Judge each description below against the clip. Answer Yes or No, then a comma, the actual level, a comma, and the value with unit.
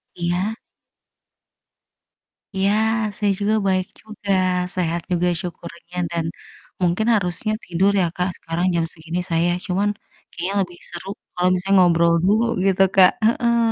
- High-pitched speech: No, medium, 180 Hz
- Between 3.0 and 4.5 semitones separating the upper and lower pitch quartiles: No, narrow, 2.5 semitones